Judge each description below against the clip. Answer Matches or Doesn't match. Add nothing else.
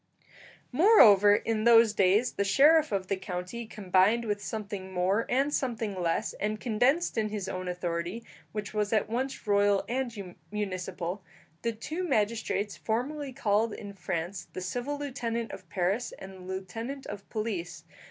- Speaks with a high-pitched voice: Matches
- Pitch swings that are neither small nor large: Matches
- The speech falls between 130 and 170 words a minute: Matches